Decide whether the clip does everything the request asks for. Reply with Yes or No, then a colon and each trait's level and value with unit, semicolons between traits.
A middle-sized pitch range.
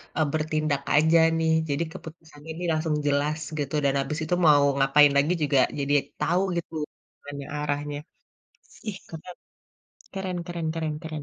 No: narrow, 2.1 semitones